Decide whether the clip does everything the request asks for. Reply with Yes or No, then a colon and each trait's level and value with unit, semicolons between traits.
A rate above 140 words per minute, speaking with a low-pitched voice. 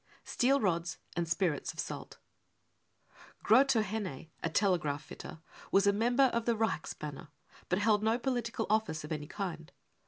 No: average, 160 wpm; high, 200 Hz